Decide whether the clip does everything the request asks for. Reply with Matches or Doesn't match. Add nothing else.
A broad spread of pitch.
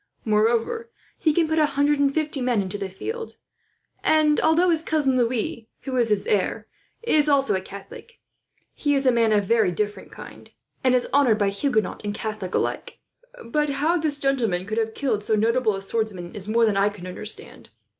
Matches